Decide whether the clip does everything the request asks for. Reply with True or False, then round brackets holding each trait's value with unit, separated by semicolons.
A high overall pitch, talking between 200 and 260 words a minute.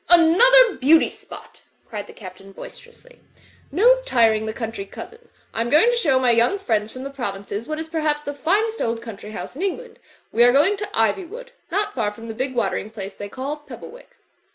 True (275 Hz; 205 wpm)